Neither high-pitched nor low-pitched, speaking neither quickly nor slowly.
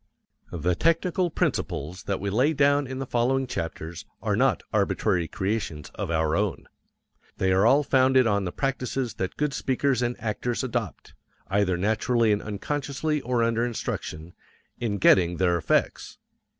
No: low, 115 Hz; average, 150 wpm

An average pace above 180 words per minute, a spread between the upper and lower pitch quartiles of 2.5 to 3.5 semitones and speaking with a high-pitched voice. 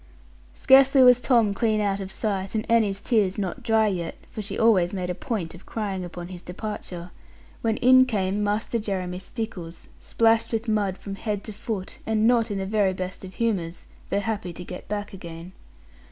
Yes: average, 190 wpm; average, 3.2 semitones; high, 205 Hz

